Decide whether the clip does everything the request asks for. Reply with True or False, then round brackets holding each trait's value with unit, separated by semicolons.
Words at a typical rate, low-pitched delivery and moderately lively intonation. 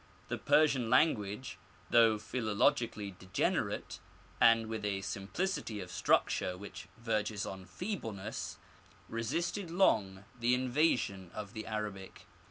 False (115 wpm; 110 Hz; 3.9 semitones)